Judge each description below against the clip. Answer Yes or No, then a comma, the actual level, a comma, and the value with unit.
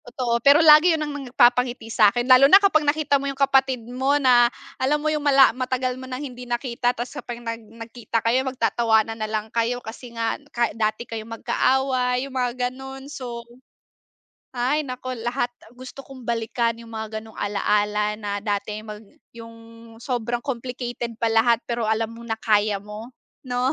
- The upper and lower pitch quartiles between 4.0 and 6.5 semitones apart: No, narrow, 2.4 semitones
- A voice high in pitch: Yes, high, 240 Hz